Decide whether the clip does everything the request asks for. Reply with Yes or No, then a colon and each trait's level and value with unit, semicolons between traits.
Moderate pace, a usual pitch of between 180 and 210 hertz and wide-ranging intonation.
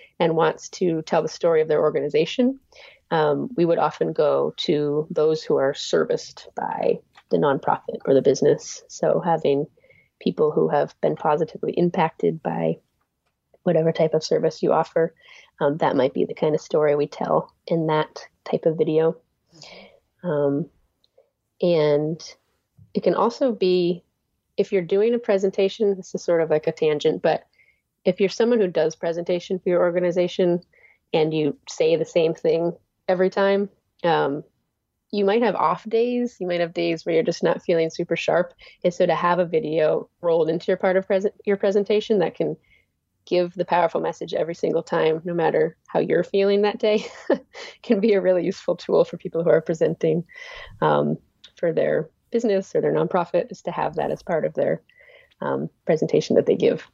Yes: average, 180 wpm; medium, 185 Hz; wide, 6.9 semitones